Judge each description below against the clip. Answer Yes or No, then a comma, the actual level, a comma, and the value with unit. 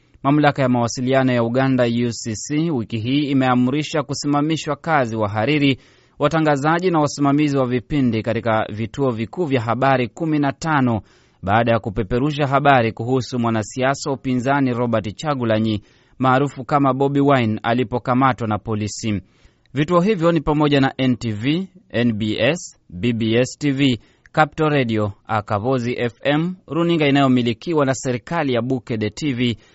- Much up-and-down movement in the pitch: No, average, 3.9 semitones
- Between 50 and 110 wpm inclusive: No, average, 120 wpm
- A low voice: Yes, low, 130 Hz